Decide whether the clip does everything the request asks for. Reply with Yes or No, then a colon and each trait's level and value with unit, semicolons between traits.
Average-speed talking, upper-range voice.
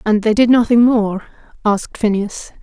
Yes: average, 160 wpm; high, 220 Hz